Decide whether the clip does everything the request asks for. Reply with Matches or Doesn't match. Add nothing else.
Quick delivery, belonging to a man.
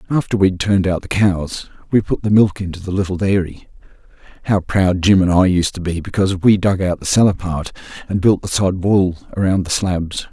Matches